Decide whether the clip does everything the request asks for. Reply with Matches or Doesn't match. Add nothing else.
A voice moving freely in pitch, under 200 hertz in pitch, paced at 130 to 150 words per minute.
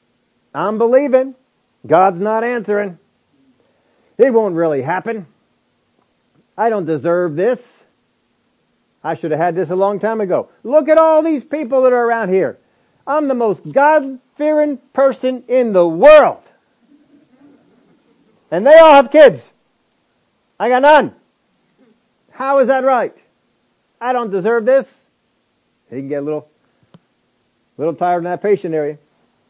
Doesn't match